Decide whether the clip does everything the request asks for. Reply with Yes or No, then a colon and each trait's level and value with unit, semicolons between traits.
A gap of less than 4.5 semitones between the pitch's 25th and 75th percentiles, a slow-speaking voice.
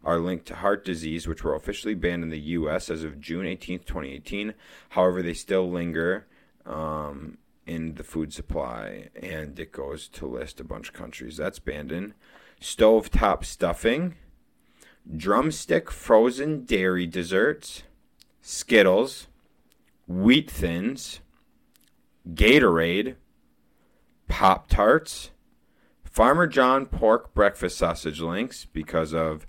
Yes: average, 3.9 semitones; slow, 120 wpm